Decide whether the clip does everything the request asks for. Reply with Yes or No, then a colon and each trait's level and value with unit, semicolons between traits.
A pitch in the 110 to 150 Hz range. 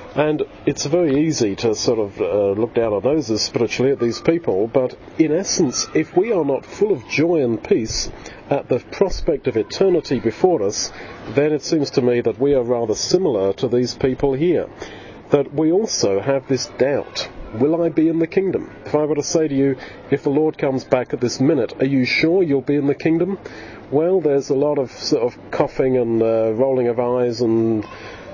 Yes: medium, 140 Hz